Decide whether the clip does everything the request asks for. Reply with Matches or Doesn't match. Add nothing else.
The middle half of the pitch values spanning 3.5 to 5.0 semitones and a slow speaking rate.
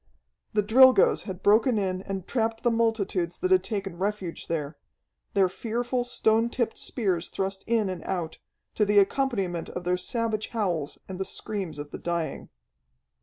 Doesn't match